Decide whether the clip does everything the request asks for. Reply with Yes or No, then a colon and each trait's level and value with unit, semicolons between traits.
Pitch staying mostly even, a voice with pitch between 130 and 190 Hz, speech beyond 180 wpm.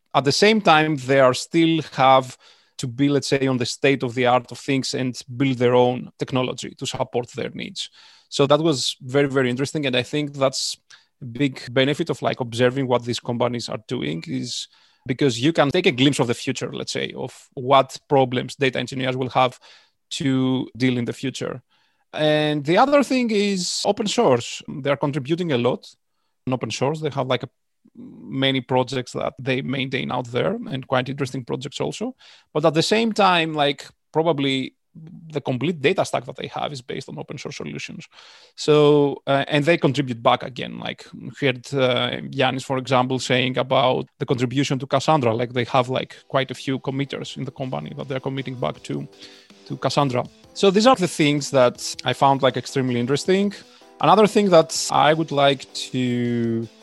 No: average, 3.1 semitones; low, 135 Hz; average, 190 wpm